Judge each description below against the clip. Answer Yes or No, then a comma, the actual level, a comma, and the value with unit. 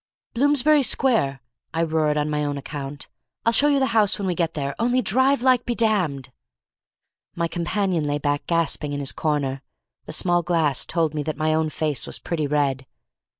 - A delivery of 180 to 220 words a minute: Yes, average, 190 wpm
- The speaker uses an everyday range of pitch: No, wide, 7.0 semitones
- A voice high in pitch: No, medium, 160 Hz